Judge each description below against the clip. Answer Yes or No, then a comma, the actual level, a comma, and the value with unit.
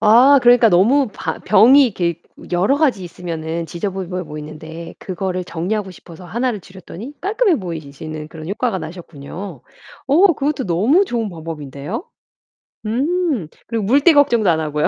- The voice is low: No, high, 190 Hz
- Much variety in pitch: Yes, wide, 7.0 semitones